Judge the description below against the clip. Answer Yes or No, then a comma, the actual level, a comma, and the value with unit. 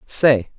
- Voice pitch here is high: No, low, 125 Hz